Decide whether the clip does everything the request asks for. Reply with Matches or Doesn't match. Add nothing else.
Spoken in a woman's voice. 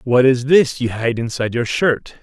Doesn't match